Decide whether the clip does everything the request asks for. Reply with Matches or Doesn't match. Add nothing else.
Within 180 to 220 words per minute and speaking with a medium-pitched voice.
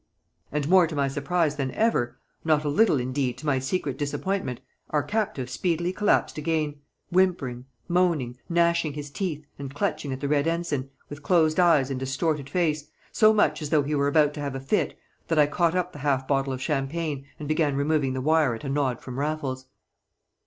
Matches